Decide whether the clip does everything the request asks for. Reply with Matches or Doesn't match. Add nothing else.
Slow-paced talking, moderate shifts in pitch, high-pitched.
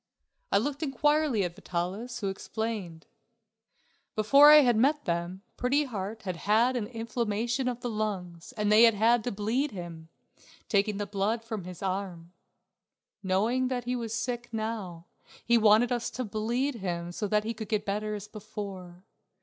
Doesn't match